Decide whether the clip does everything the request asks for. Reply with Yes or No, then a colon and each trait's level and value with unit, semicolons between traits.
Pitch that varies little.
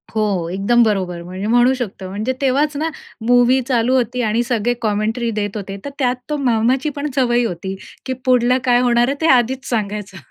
No: average, 3.6 semitones